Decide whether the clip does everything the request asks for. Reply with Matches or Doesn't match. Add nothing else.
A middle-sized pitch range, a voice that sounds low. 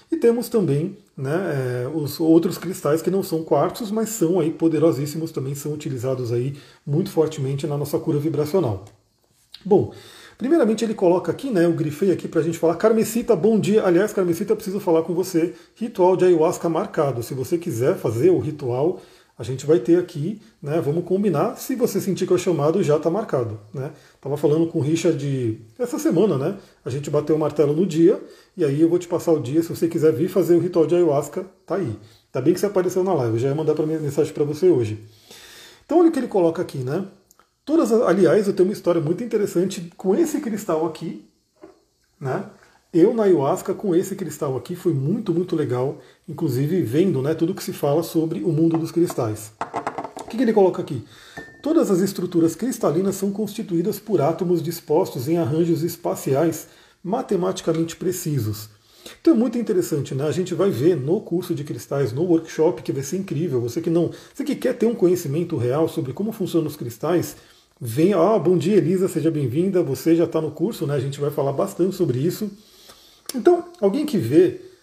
Doesn't match